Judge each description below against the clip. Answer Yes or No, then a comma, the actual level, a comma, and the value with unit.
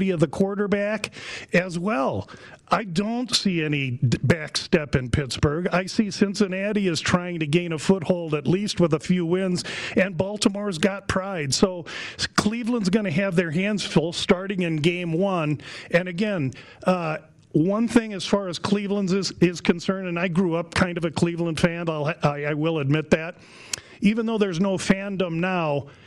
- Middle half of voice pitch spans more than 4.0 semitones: No, average, 3.4 semitones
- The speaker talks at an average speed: Yes, average, 175 wpm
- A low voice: No, medium, 180 Hz